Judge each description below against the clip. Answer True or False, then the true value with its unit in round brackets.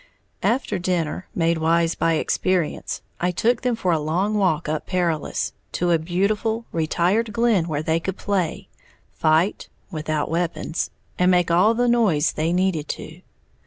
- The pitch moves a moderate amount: True (3.7 semitones)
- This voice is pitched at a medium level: True (175 Hz)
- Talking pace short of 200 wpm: True (155 wpm)